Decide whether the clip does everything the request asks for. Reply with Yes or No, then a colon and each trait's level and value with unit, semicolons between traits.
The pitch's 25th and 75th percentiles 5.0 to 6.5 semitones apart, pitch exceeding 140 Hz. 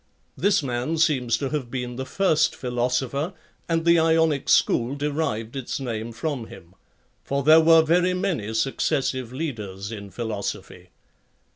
No: average, 5.3 semitones; low, 135 Hz